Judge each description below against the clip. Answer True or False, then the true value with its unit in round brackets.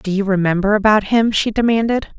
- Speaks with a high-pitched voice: True (210 Hz)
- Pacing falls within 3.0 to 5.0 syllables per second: False (5.6 syllables/s)